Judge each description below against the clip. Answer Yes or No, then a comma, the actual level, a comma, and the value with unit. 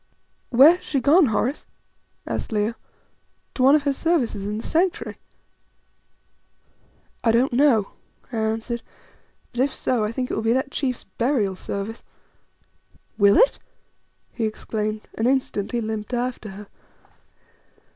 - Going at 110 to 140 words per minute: Yes, slow, 135 wpm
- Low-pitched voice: No, high, 235 Hz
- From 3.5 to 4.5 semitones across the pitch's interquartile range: Yes, average, 3.8 semitones